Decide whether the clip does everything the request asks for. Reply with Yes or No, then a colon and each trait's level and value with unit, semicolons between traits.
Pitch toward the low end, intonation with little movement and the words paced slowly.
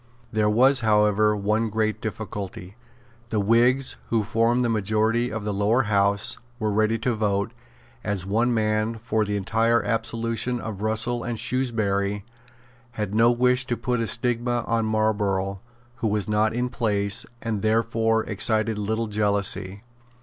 No: low, 110 Hz; narrow, 2.0 semitones; average, 150 wpm